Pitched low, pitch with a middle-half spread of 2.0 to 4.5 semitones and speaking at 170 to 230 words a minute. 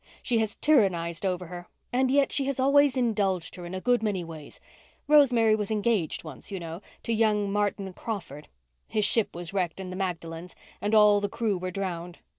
No: high, 200 Hz; average, 4.2 semitones; average, 190 wpm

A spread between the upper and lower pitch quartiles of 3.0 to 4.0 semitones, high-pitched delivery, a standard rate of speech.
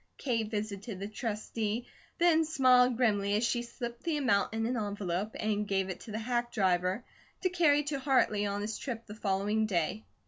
Yes: average, 3.4 semitones; high, 220 Hz; average, 185 wpm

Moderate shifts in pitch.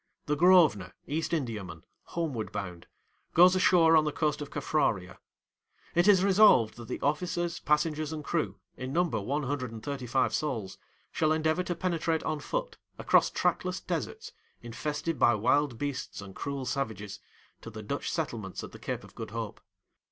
No: wide, 6.0 semitones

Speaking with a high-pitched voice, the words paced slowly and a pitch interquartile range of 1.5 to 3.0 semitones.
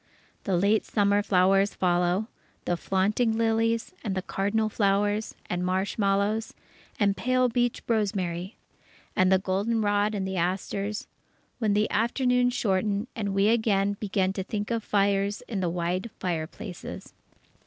Yes: high, 200 Hz; slow, 130 wpm; narrow, 2.6 semitones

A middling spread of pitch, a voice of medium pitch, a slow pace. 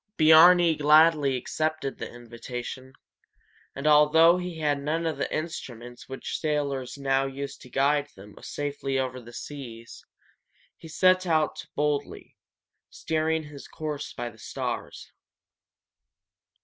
Yes: average, 3.0 semitones; medium, 145 Hz; slow, 125 wpm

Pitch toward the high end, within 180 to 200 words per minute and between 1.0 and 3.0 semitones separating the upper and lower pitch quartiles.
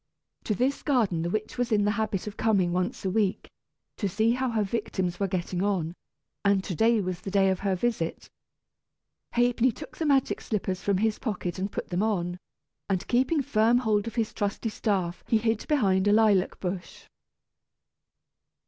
No: high, 205 Hz; average, 185 wpm; average, 3.4 semitones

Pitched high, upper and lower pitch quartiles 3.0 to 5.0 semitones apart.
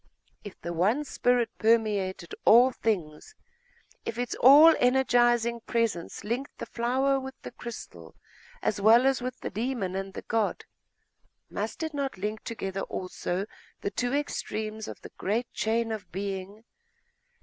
Yes: high, 225 Hz; average, 3.9 semitones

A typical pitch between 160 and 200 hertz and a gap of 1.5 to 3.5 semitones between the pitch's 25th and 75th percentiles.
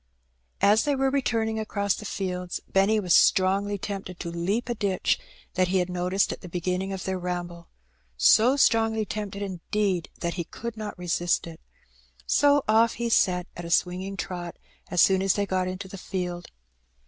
Yes: high, 190 Hz; average, 3.1 semitones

